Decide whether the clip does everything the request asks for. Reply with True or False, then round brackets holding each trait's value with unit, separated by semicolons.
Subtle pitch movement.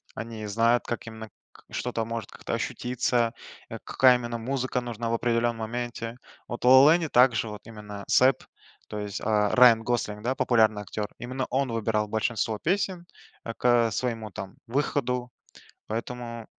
True (2.0 semitones)